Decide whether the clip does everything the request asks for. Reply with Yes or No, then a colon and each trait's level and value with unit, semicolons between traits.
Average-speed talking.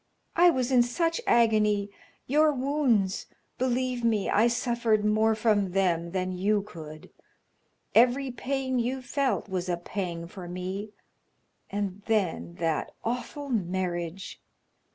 No: slow, 125 wpm